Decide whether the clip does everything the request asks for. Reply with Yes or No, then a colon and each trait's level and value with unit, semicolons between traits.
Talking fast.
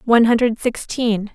No: slow, 135 wpm